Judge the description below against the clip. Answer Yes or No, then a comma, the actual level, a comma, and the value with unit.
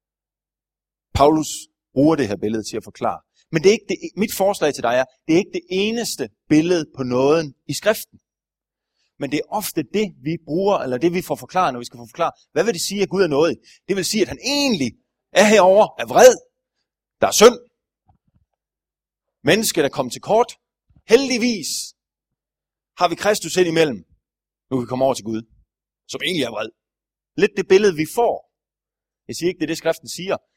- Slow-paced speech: No, average, 200 wpm